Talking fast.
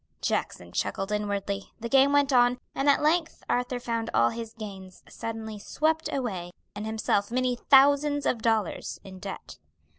No: average, 155 wpm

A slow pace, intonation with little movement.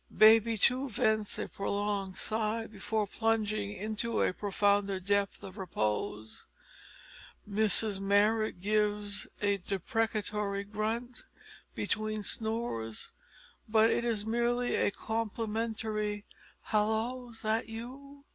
Yes: slow, 105 wpm; narrow, 1.9 semitones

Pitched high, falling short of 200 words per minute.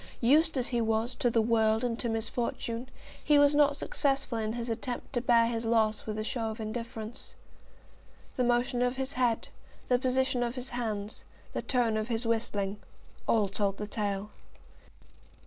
Yes: high, 235 Hz; average, 175 wpm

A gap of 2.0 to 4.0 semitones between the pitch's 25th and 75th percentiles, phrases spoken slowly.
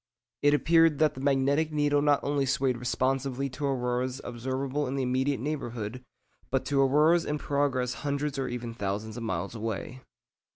No: narrow, 2.6 semitones; average, 165 wpm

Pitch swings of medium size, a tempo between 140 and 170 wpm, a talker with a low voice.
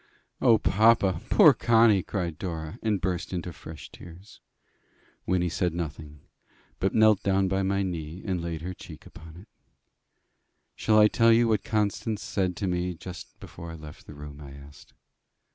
Yes: average, 3.8 semitones; average, 165 wpm; very low, 90 Hz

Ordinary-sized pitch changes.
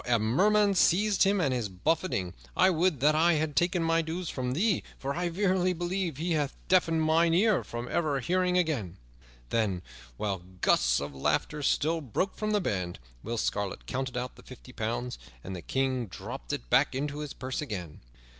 No: wide, 7.0 semitones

